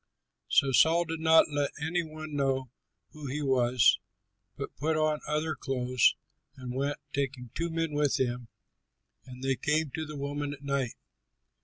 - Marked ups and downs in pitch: No, average, 2.9 semitones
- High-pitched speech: No, medium, 145 Hz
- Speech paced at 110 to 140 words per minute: No, average, 160 wpm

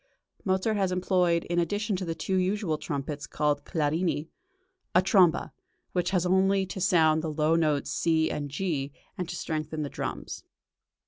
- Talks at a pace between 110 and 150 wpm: No, average, 165 wpm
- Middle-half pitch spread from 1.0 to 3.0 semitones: No, average, 3.4 semitones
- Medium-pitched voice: Yes, medium, 170 Hz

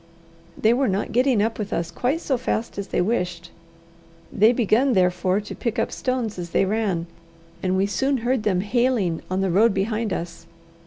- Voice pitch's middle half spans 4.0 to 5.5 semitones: Yes, average, 4.3 semitones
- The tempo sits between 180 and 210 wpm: Yes, average, 190 wpm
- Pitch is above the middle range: Yes, high, 210 Hz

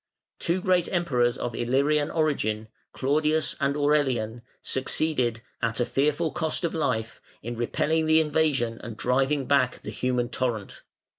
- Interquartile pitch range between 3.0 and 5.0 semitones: Yes, average, 4.5 semitones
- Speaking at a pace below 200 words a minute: Yes, average, 140 wpm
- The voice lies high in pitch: No, low, 135 Hz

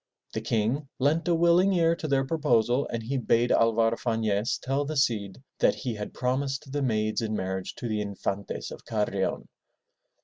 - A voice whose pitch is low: Yes, low, 120 Hz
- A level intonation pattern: No, average, 4.6 semitones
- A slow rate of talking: No, average, 175 wpm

